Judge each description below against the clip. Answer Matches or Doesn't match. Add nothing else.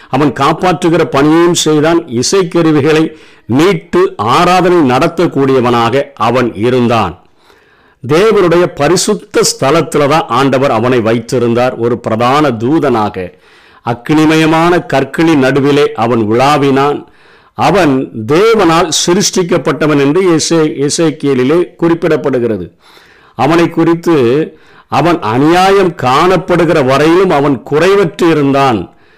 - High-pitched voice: Doesn't match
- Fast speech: Doesn't match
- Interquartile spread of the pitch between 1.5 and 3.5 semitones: Doesn't match